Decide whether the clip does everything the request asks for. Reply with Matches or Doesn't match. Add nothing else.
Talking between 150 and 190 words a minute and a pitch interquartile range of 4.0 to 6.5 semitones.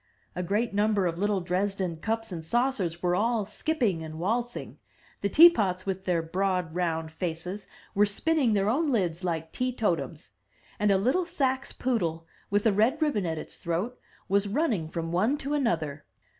Matches